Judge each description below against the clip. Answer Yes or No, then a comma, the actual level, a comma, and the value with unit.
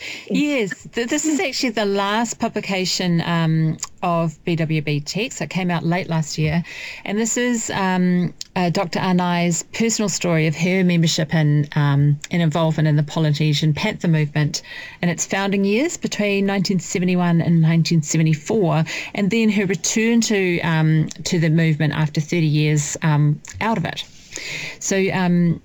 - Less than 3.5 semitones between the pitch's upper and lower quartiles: No, average, 3.9 semitones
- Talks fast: No, average, 155 wpm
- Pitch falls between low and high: Yes, medium, 175 Hz